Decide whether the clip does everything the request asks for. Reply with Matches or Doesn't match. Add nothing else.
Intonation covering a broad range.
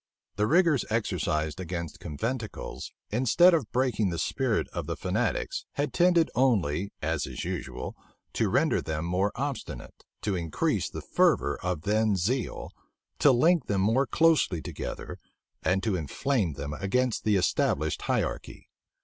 Matches